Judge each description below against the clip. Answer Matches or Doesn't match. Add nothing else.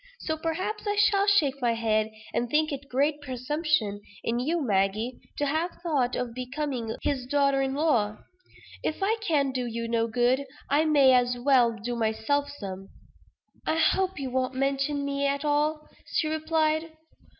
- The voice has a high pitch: Matches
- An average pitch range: Matches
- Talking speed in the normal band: Matches